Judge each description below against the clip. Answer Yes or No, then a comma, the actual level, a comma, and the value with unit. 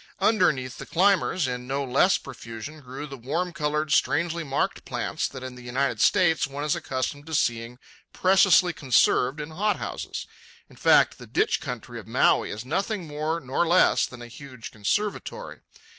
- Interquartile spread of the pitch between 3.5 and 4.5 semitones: No, average, 5.2 semitones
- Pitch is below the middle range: No, medium, 145 Hz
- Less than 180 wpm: Yes, average, 170 wpm